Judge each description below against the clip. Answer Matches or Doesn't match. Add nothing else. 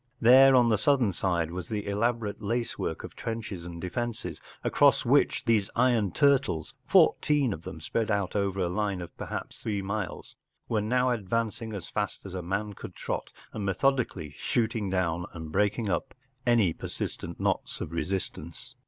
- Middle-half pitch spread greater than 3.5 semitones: Matches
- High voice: Doesn't match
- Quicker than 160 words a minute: Matches